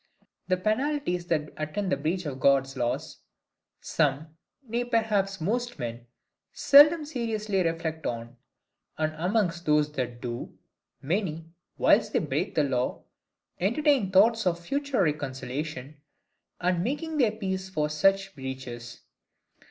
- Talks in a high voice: No, medium, 170 Hz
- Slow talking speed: Yes, slow, 125 wpm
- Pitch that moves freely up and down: Yes, wide, 7.0 semitones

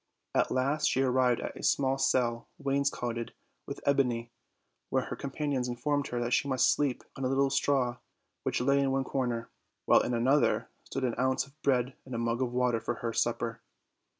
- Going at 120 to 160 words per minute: No, average, 190 wpm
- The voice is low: Yes, low, 130 Hz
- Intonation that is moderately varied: No, narrow, 2.3 semitones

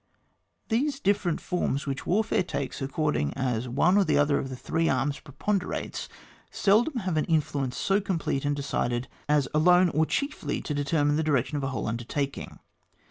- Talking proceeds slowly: No, average, 165 wpm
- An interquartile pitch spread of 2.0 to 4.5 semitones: No, average, 4.9 semitones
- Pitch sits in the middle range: Yes, medium, 150 Hz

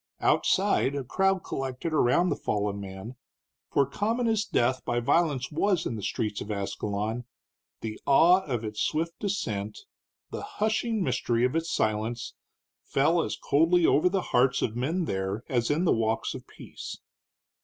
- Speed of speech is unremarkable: Yes, average, 160 wpm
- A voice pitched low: Yes, low, 130 Hz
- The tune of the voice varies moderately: No, wide, 7.5 semitones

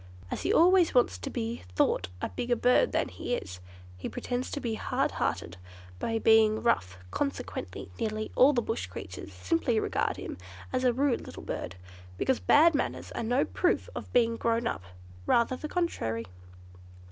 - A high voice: Yes, high, 235 Hz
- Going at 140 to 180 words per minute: Yes, average, 170 wpm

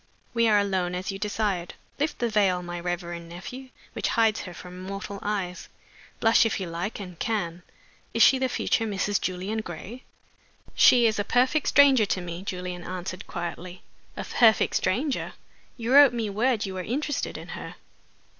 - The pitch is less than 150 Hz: No, high, 200 Hz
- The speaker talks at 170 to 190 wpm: Yes, average, 175 wpm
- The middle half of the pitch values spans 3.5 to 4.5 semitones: Yes, average, 4.2 semitones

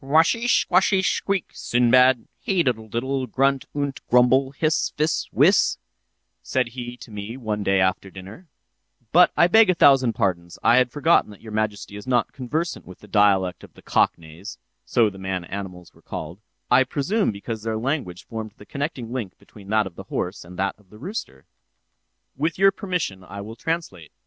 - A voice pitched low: Yes, low, 115 Hz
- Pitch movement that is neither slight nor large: No, wide, 6.1 semitones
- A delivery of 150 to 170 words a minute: No, average, 180 wpm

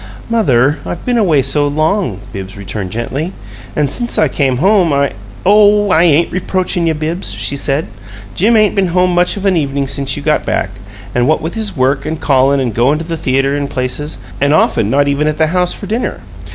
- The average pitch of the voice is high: No, medium, 150 Hz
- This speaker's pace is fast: Yes, fast, 210 wpm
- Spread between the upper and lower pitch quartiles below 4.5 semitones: No, average, 4.9 semitones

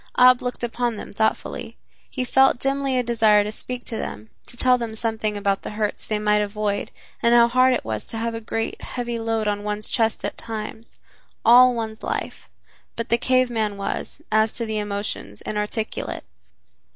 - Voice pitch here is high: Yes, high, 225 Hz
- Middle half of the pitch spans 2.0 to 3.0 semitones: Yes, narrow, 2.4 semitones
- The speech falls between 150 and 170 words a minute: No, average, 190 wpm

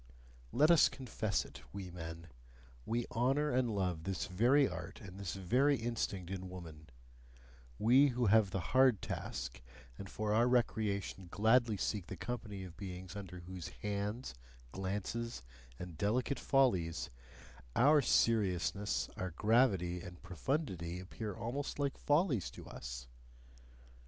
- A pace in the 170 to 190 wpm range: No, slow, 135 wpm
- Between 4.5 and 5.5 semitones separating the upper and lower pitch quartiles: Yes, average, 5.1 semitones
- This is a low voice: Yes, low, 100 Hz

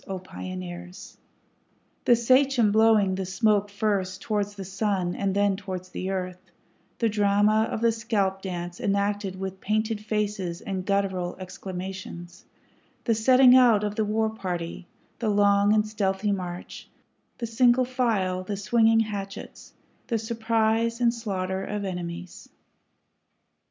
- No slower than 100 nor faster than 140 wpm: Yes, slow, 135 wpm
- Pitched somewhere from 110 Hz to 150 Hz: No, high, 205 Hz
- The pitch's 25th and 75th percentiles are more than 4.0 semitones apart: No, average, 2.8 semitones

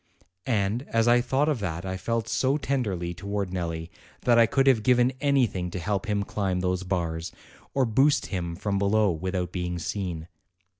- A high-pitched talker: No, low, 100 Hz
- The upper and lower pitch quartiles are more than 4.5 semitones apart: Yes, average, 5.0 semitones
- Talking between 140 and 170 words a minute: No, average, 180 wpm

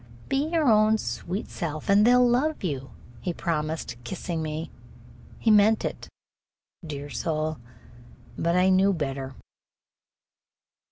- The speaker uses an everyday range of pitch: No, wide, 5.9 semitones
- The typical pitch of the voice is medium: Yes, medium, 175 Hz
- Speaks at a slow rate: Yes, slow, 125 wpm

